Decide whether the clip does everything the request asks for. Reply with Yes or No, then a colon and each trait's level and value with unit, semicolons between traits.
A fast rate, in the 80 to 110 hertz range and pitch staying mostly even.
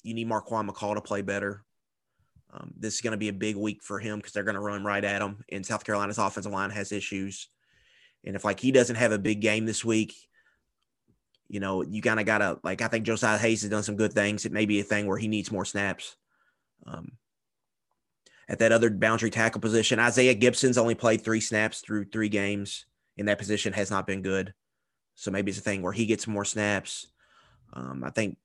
Yes: fast, 225 wpm; low, 105 Hz; narrow, 1.8 semitones